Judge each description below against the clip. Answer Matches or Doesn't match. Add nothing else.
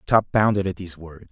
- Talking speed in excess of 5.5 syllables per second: Matches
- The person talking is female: Doesn't match